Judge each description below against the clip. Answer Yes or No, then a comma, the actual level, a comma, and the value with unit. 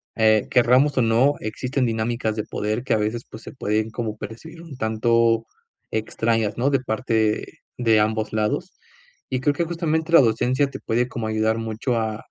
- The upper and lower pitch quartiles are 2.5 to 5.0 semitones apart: Yes, average, 2.8 semitones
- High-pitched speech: No, low, 115 Hz